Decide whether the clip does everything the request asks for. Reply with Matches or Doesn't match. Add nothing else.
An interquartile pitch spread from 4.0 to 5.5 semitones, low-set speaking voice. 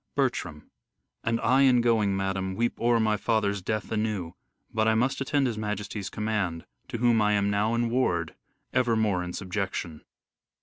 Doesn't match